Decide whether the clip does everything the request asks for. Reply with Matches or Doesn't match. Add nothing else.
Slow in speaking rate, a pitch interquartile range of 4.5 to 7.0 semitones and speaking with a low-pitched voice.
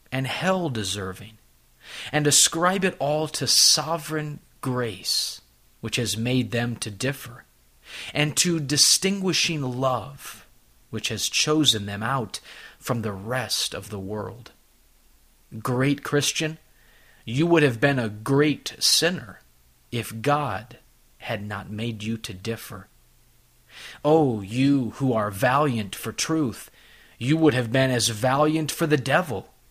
Matches